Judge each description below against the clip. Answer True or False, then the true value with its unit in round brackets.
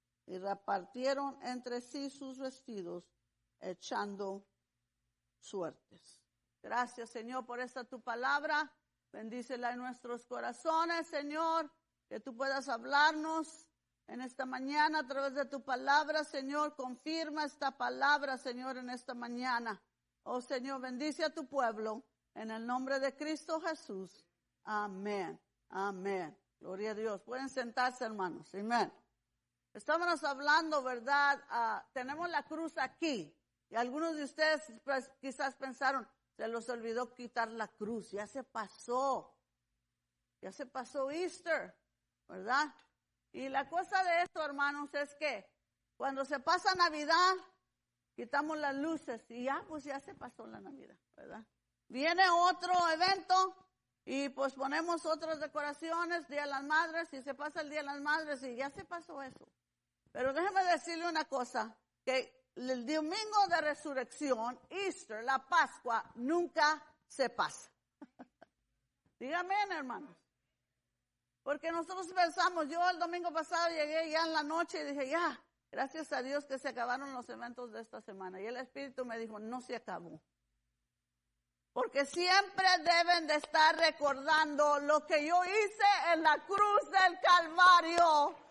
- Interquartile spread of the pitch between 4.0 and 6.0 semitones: True (4.6 semitones)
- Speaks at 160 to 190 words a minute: False (140 wpm)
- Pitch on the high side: True (280 Hz)